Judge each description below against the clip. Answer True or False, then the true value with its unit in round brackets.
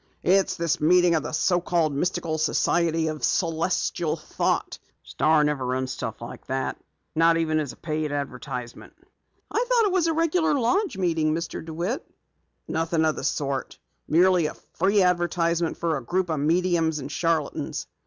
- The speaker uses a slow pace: False (165 wpm)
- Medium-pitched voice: True (165 Hz)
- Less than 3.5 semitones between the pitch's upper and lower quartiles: True (2.7 semitones)